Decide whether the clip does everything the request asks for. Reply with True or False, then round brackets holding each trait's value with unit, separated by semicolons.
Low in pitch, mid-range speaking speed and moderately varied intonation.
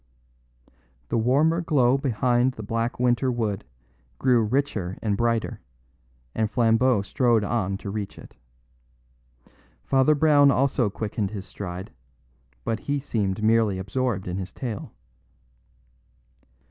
False (115 Hz; 120 wpm; 4.1 semitones)